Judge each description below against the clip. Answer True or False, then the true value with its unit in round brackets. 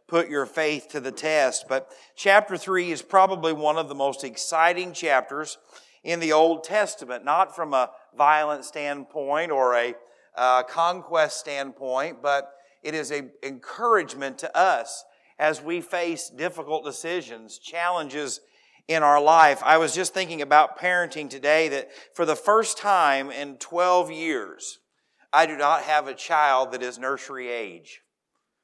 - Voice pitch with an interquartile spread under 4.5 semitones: True (3.7 semitones)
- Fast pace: False (150 wpm)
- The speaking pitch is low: False (155 Hz)